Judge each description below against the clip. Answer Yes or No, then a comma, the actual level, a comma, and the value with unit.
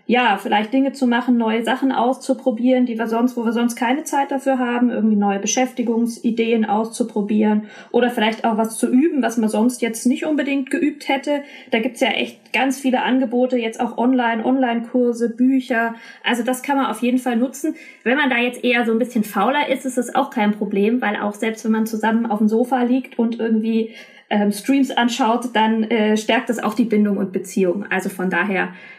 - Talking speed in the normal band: No, fast, 205 wpm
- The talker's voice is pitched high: Yes, high, 240 Hz